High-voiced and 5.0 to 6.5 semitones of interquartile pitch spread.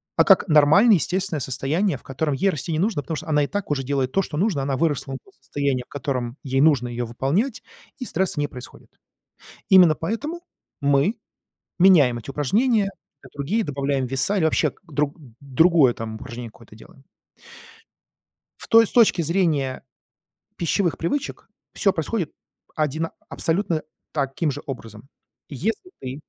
No: medium, 150 Hz; wide, 5.6 semitones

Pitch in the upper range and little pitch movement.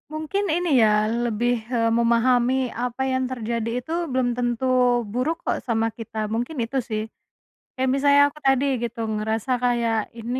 Yes: high, 240 Hz; narrow, 2.3 semitones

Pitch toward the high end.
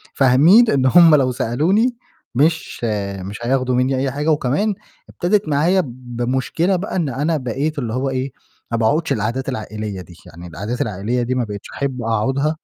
No: low, 130 Hz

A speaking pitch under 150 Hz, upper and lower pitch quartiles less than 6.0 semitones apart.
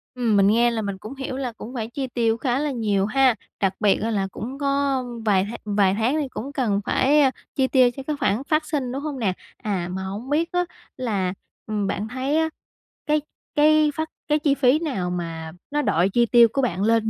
No: high, 240 Hz; average, 5.3 semitones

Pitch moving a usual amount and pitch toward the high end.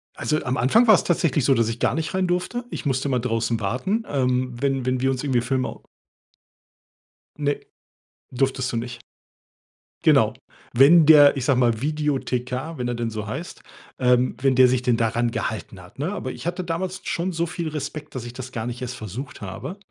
No: average, 4.0 semitones; low, 130 Hz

